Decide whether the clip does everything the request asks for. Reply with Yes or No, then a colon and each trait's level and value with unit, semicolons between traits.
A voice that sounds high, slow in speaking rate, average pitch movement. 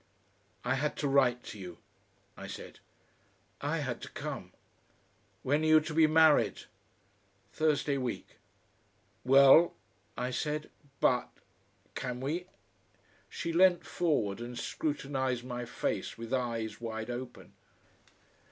No: low, 135 Hz; slow, 120 wpm; average, 3.9 semitones